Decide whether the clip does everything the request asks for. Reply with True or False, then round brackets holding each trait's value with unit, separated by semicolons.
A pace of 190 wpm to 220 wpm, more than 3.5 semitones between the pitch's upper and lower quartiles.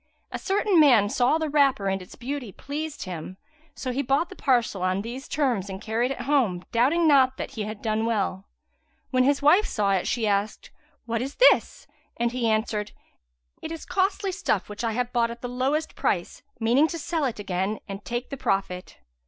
True (195 wpm; 5.5 semitones)